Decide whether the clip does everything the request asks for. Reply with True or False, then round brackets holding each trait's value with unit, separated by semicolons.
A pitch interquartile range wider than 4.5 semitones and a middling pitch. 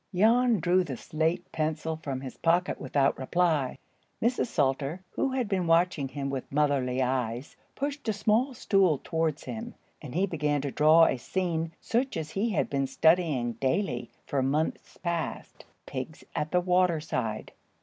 True (5.1 semitones; 160 Hz)